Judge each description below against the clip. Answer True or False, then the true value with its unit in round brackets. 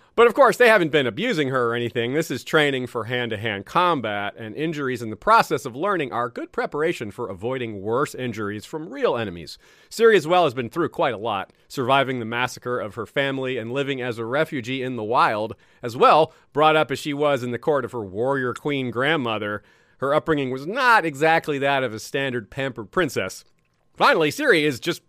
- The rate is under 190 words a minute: False (205 wpm)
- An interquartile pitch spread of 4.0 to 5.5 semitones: True (4.6 semitones)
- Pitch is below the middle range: True (130 Hz)